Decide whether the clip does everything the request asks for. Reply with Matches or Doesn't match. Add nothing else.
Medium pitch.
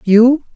Doesn't match